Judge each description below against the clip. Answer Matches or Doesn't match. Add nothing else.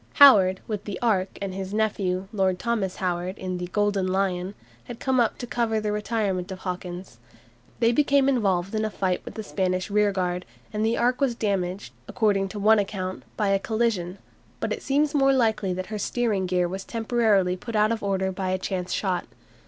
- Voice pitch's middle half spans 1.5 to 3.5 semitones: Matches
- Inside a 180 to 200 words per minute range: Matches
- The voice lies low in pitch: Doesn't match